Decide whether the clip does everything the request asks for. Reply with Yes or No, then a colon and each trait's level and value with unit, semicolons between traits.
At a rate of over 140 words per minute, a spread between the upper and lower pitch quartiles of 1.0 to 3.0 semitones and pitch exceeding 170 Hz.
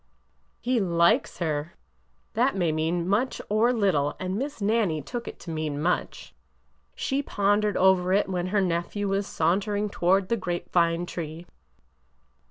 No: average, 150 wpm; average, 3.4 semitones; medium, 185 Hz